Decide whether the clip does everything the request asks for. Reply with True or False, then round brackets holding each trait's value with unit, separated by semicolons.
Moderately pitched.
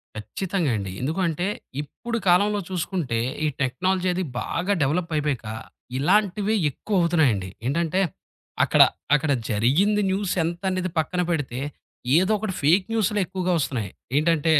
True (175 Hz)